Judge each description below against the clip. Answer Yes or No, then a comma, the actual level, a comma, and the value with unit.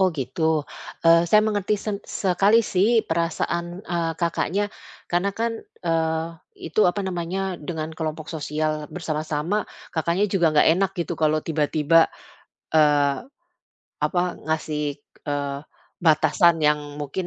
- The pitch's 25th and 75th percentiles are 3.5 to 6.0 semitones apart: No, average, 2.9 semitones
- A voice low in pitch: No, medium, 165 Hz